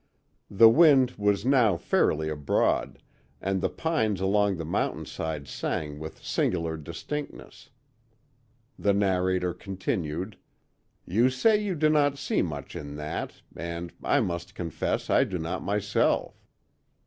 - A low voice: Yes, very low, 95 Hz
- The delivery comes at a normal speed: No, slow, 125 wpm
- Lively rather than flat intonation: Yes, wide, 5.8 semitones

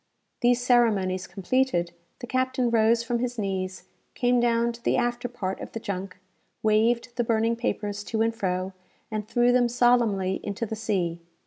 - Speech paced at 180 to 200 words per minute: No, average, 165 wpm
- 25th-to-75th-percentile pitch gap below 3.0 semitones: No, average, 3.5 semitones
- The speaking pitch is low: No, high, 230 Hz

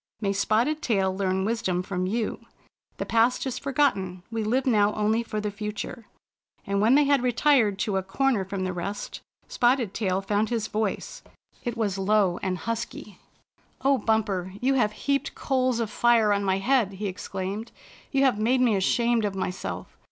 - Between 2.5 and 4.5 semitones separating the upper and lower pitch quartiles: Yes, average, 3.8 semitones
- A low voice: No, high, 215 Hz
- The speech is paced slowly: No, average, 180 wpm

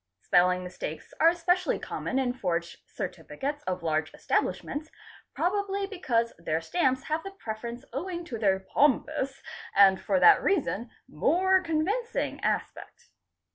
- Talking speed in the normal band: No, slow, 130 wpm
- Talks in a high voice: Yes, very high, 275 Hz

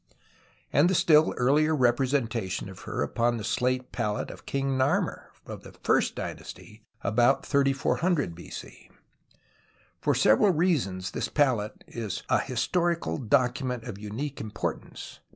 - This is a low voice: Yes, low, 125 Hz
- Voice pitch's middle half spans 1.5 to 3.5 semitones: No, average, 4.9 semitones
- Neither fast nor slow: No, slow, 130 wpm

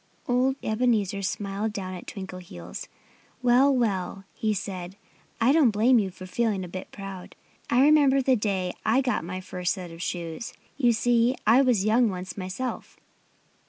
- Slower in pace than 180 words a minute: Yes, average, 160 wpm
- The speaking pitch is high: Yes, high, 210 Hz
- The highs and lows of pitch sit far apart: No, average, 4.8 semitones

